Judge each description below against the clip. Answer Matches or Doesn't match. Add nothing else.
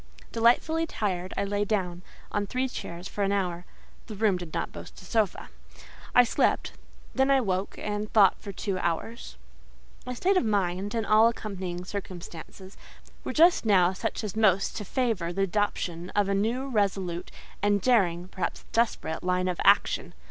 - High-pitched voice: Matches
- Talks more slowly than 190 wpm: Matches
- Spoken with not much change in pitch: Doesn't match